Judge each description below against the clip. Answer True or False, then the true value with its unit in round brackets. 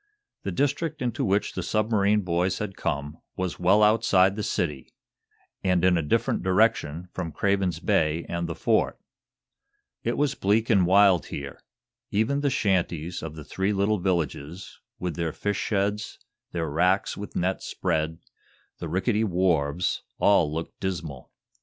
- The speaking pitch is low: True (95 Hz)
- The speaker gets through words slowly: False (155 wpm)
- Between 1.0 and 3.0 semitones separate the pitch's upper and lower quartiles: False (3.6 semitones)